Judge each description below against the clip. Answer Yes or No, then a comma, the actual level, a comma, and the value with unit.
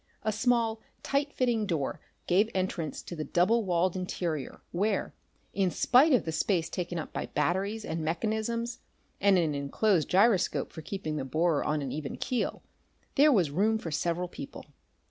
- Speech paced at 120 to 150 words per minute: No, average, 165 wpm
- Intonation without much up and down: No, average, 5.3 semitones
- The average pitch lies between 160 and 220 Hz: Yes, medium, 185 Hz